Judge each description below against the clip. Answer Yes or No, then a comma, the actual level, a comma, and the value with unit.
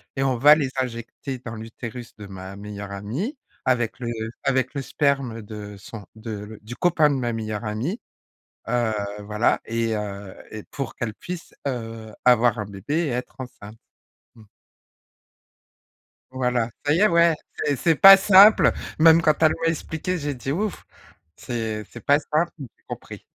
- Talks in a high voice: No, low, 120 Hz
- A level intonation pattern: No, average, 5.2 semitones